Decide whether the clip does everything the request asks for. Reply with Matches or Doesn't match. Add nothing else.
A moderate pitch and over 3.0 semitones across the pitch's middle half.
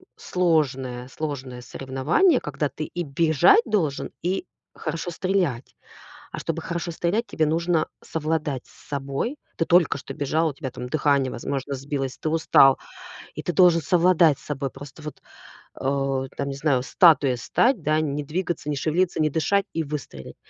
Matches